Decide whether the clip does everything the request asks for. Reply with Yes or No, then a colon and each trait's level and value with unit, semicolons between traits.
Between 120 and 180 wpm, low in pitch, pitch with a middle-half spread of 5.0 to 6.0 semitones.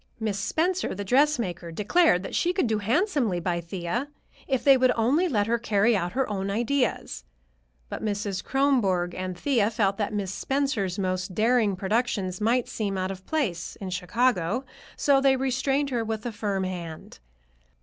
No: average, 170 wpm; high, 215 Hz; wide, 5.5 semitones